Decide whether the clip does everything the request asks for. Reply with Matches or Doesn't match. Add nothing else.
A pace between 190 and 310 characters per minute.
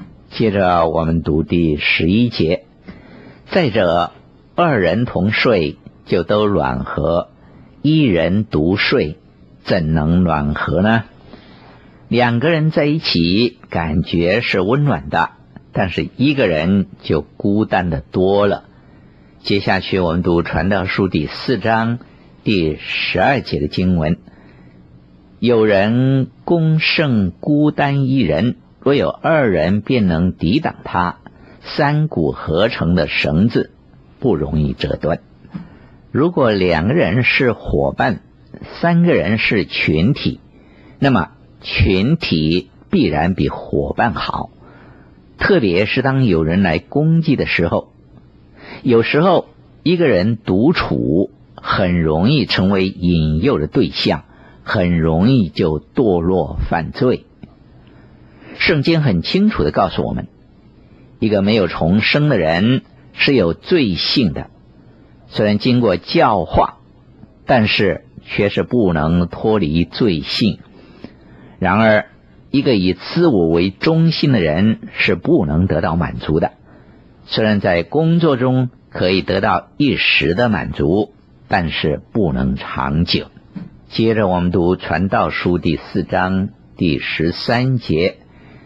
Doesn't match